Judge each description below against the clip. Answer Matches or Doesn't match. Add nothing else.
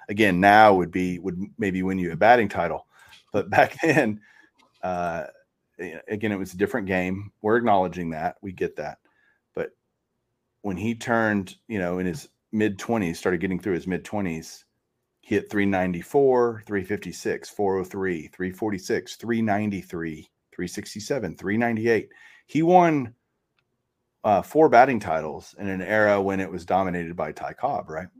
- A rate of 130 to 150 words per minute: Matches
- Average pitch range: Matches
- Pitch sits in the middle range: Doesn't match